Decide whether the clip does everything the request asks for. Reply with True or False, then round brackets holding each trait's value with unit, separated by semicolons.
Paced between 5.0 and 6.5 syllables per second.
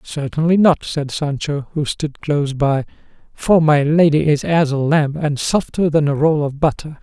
False (4.5 syllables/s)